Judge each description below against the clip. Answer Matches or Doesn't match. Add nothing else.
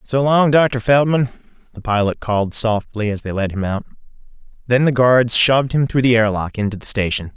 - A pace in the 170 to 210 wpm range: Matches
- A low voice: Matches